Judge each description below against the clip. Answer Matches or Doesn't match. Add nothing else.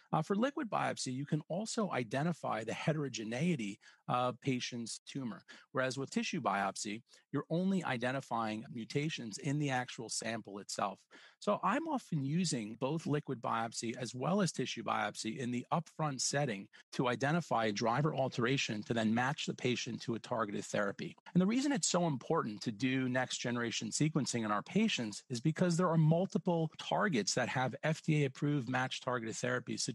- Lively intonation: Matches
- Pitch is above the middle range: Doesn't match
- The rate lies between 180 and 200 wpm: Doesn't match